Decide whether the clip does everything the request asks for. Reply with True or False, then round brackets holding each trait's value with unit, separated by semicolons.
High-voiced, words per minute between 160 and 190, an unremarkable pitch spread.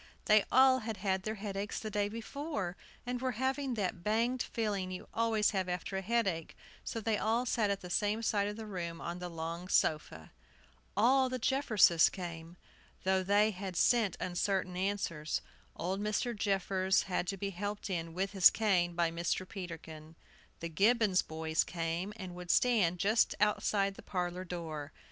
True (195 Hz; 170 wpm; 3.7 semitones)